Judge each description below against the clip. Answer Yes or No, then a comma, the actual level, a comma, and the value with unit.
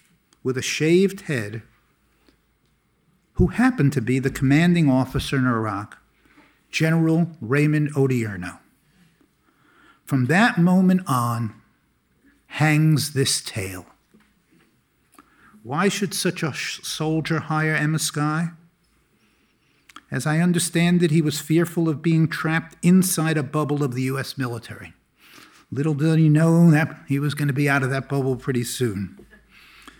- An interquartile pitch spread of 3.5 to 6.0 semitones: Yes, average, 3.9 semitones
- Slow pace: Yes, slow, 130 wpm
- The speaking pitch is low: No, medium, 150 Hz